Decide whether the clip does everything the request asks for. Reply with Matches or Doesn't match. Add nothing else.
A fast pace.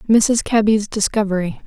Doesn't match